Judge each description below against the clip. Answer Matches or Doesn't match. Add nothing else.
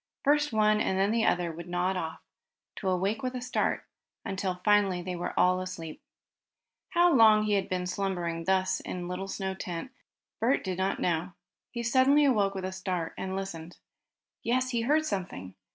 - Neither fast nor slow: Matches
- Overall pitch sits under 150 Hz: Doesn't match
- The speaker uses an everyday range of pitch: Matches